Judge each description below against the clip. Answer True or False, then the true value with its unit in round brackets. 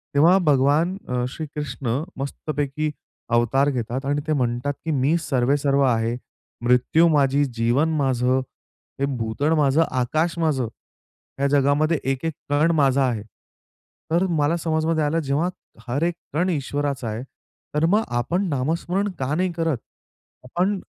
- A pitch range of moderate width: True (3.7 semitones)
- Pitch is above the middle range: False (145 Hz)